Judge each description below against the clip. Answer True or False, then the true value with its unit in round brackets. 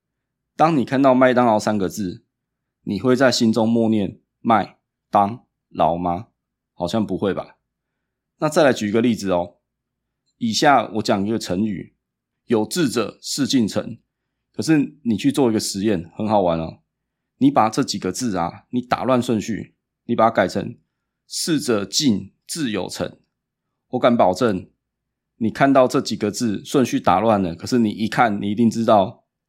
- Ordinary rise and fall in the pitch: True (3.5 semitones)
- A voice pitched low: True (110 Hz)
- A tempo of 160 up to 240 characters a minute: True (225 characters per minute)